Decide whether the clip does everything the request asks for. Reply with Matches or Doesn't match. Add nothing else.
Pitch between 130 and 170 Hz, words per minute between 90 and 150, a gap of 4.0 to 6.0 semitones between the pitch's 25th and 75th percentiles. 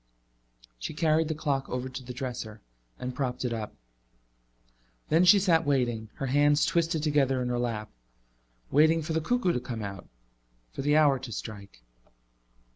Doesn't match